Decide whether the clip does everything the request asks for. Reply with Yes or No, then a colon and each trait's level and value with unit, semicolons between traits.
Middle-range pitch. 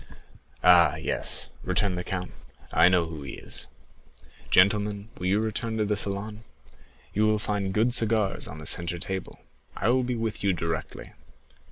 No: low, 100 Hz